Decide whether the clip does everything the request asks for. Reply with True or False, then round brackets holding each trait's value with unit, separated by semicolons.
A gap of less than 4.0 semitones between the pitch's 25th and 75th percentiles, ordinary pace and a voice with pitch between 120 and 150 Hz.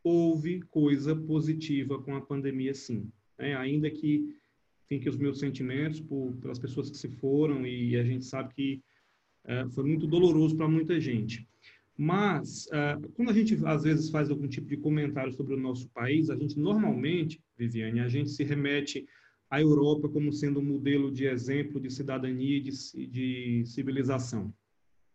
True (2.5 semitones; 170 wpm; 140 Hz)